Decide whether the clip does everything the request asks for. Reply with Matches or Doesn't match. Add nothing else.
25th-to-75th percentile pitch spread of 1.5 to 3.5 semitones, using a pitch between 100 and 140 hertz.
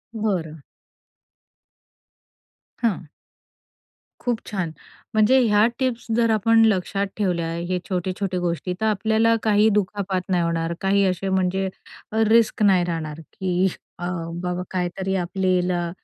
Doesn't match